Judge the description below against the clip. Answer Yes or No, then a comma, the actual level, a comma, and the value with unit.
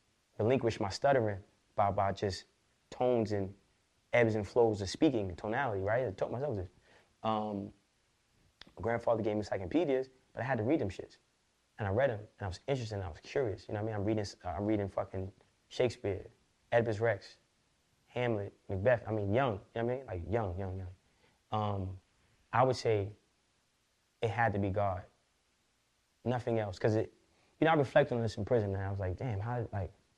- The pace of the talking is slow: No, average, 200 wpm